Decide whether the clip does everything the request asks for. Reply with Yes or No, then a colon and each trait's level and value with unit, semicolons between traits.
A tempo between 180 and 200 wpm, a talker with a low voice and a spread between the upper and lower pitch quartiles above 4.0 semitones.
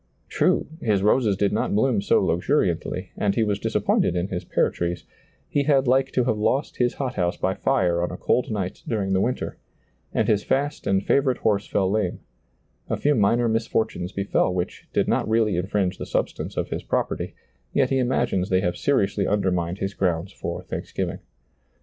Yes: average, 190 wpm; low, 100 Hz; average, 4.6 semitones